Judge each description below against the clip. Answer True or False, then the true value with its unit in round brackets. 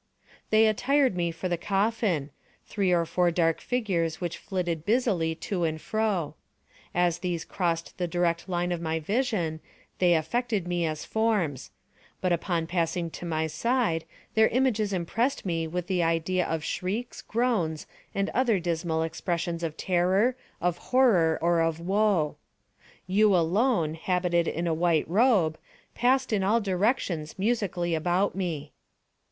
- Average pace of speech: True (145 wpm)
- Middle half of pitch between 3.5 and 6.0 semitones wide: True (4.2 semitones)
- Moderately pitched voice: True (175 Hz)